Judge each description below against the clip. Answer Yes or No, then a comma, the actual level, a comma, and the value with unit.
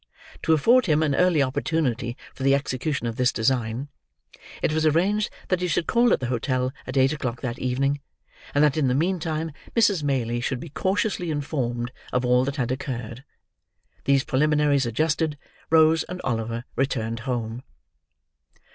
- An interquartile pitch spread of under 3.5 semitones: No, average, 4.1 semitones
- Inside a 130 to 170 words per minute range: Yes, average, 165 wpm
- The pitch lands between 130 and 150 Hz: Yes, medium, 140 Hz